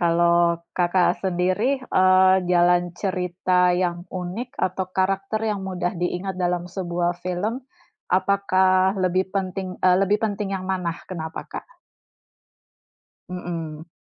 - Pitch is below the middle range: No, medium, 185 Hz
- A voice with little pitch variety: Yes, narrow, 1.4 semitones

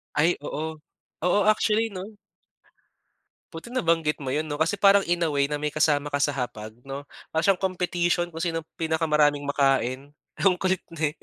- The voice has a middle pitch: Yes, medium, 160 Hz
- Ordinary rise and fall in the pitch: Yes, average, 3.5 semitones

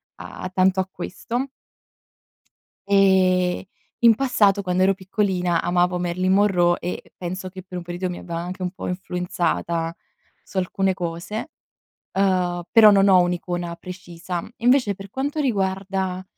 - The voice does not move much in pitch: Yes, narrow, 1.8 semitones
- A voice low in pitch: No, medium, 185 Hz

